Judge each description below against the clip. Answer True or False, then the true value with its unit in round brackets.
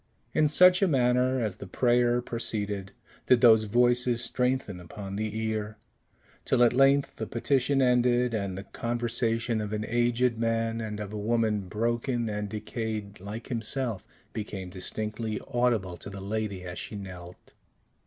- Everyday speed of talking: True (155 wpm)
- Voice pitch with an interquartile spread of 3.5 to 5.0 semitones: False (2.8 semitones)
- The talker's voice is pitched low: True (115 Hz)